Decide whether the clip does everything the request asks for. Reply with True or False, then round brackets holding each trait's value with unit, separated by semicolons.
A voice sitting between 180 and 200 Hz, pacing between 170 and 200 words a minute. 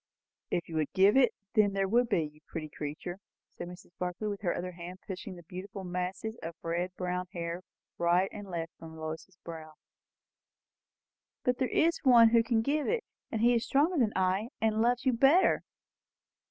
True (190 Hz; 180 wpm)